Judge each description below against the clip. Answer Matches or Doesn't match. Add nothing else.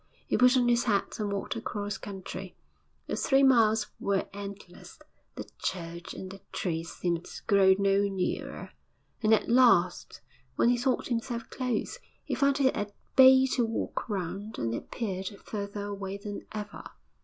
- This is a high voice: Matches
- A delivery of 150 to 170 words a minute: Matches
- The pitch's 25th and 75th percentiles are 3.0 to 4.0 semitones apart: Matches